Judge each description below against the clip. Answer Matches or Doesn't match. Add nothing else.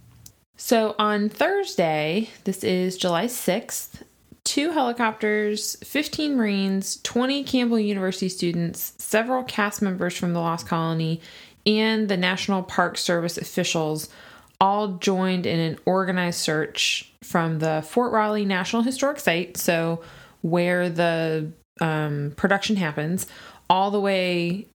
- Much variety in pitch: Doesn't match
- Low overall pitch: Doesn't match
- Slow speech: Matches